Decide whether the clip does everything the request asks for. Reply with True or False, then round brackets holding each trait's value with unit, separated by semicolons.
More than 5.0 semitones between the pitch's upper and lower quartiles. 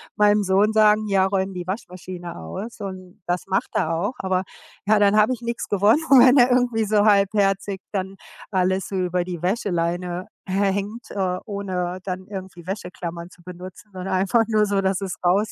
False (2.4 semitones)